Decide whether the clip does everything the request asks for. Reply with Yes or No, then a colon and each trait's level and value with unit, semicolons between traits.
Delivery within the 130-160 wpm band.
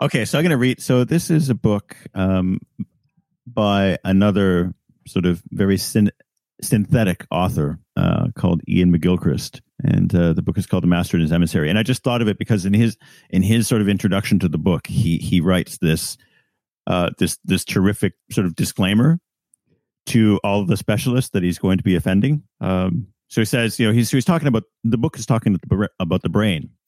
No: fast, 205 wpm